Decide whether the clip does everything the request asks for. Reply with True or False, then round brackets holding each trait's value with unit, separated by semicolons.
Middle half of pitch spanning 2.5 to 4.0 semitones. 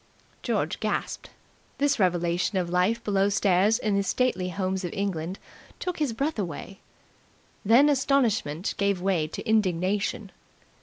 True (3.6 semitones)